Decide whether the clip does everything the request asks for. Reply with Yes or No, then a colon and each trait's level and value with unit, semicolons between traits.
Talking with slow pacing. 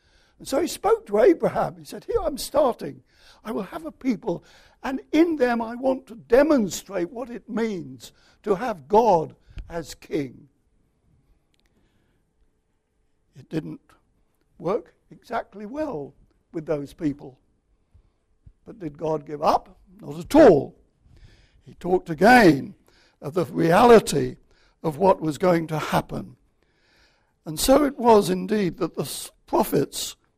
Yes: slow, 130 wpm